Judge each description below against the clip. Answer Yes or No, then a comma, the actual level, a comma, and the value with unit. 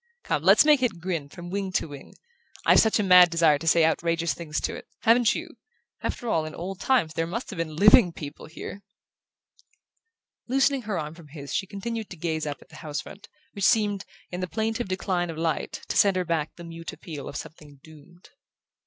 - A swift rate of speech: Yes, fast, 210 wpm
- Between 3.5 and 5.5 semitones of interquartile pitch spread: Yes, average, 4.2 semitones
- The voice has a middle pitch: Yes, medium, 175 Hz